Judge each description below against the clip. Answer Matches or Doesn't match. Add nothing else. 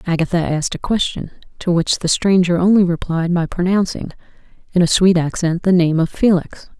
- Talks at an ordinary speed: Matches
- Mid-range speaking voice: Matches